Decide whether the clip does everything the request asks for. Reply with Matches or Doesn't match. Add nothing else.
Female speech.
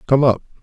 Doesn't match